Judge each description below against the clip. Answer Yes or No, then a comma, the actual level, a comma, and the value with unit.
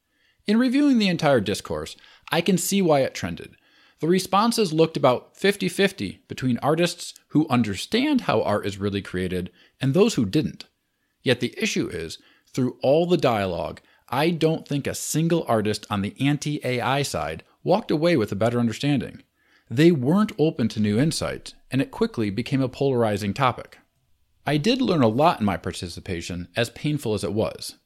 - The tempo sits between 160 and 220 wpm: Yes, average, 175 wpm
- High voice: No, medium, 140 Hz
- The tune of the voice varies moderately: No, wide, 8.1 semitones